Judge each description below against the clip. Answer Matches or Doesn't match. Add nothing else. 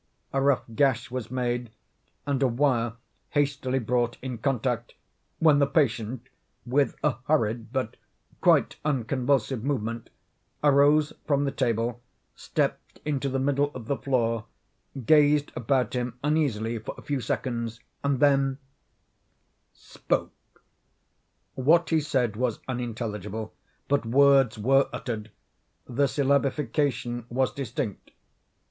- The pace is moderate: Doesn't match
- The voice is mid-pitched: Doesn't match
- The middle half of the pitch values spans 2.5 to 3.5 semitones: Matches